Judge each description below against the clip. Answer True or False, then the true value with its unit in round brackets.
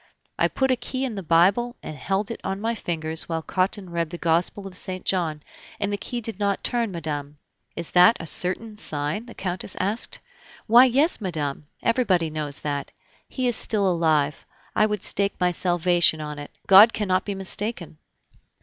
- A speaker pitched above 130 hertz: True (185 Hz)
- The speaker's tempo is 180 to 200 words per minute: True (185 wpm)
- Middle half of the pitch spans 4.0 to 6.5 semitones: True (4.8 semitones)